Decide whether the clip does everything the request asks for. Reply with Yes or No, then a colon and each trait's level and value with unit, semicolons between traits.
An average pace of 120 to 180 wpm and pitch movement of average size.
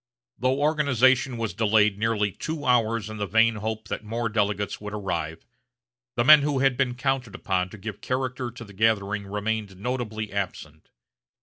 Yes: average, 170 wpm; average, 3.5 semitones